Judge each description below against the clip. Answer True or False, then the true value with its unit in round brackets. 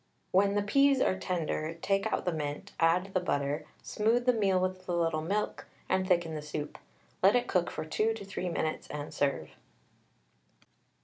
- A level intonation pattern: False (4.3 semitones)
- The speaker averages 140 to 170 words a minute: False (180 wpm)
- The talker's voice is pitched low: False (185 Hz)